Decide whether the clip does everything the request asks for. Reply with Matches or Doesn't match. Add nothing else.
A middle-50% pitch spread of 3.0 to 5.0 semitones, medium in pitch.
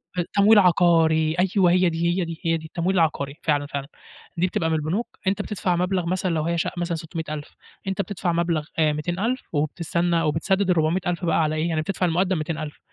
Doesn't match